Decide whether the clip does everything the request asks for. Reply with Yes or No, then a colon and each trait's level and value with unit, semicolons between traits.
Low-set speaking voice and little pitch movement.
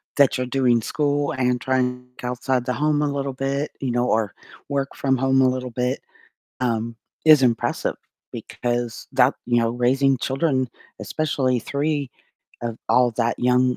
Yes: low, 130 Hz; narrow, 1.9 semitones